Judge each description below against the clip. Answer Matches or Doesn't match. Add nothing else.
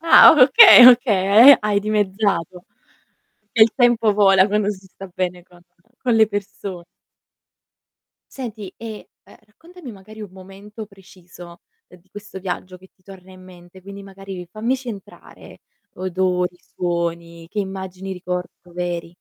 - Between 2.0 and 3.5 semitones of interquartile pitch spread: Matches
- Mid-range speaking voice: Doesn't match